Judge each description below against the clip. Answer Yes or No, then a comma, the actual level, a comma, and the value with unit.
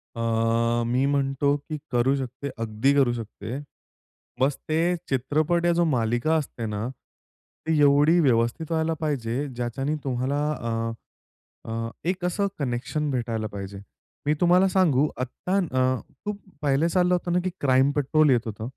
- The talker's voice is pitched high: No, medium, 140 Hz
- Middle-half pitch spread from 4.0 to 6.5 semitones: Yes, average, 4.5 semitones